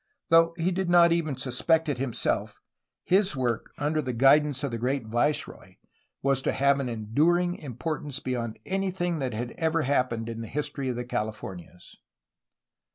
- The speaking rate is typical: Yes, average, 165 wpm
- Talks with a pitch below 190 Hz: Yes, medium, 140 Hz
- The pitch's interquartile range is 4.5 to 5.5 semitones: Yes, average, 5.1 semitones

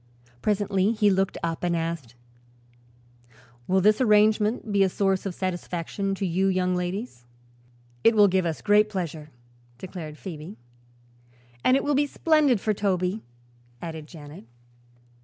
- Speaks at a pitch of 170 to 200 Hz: Yes, high, 190 Hz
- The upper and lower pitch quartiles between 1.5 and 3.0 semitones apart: No, average, 3.5 semitones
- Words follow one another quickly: No, average, 140 wpm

